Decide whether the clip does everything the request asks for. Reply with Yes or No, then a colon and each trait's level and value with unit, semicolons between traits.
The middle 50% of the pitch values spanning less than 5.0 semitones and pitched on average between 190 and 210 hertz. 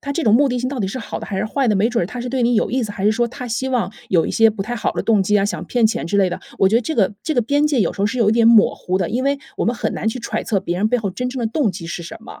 No: average, 3.7 semitones; high, 225 Hz